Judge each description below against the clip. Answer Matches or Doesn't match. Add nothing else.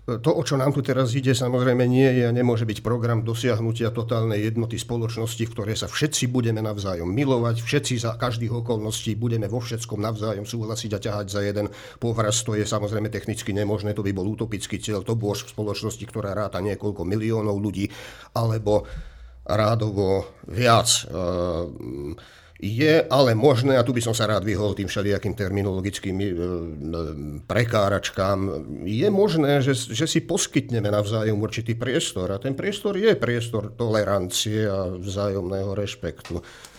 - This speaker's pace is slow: Doesn't match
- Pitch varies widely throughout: Doesn't match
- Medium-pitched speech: Doesn't match